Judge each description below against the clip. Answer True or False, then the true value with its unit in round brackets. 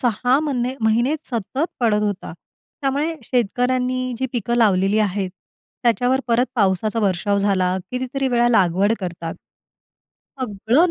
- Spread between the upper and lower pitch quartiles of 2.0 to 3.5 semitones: False (4.1 semitones)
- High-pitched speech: True (235 Hz)